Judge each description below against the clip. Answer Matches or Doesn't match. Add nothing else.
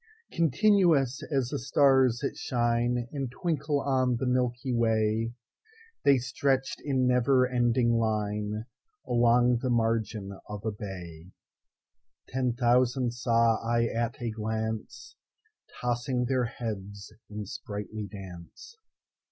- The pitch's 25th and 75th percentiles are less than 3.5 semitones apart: Matches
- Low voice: Matches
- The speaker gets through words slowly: Matches